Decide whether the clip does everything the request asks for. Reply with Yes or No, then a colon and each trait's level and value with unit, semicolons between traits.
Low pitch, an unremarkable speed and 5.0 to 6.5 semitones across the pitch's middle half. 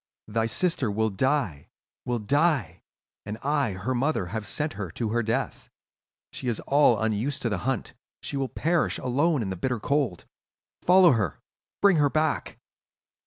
Yes: low, 125 Hz; average, 165 wpm; wide, 5.4 semitones